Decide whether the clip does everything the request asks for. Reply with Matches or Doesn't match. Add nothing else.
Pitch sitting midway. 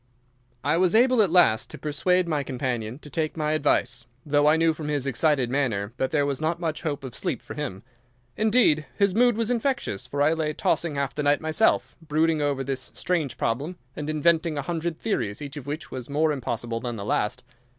Matches